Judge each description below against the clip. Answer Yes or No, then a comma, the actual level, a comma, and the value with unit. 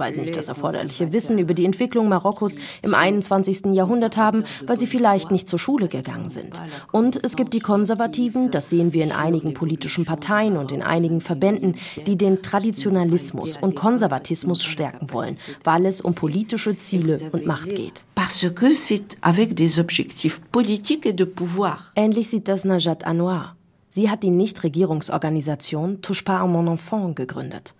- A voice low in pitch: No, high, 190 Hz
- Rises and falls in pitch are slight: No, average, 4.0 semitones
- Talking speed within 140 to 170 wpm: Yes, average, 145 wpm